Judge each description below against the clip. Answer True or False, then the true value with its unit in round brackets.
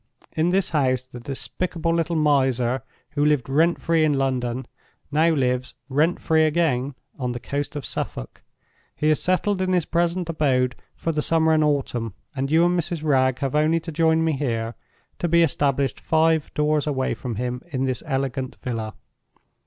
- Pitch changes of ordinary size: True (3.9 semitones)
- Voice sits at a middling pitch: True (150 Hz)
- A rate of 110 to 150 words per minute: False (175 wpm)